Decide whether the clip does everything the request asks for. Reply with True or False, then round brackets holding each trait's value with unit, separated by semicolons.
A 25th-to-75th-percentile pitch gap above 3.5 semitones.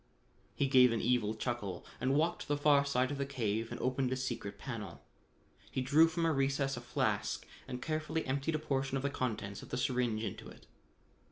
False (2.8 semitones)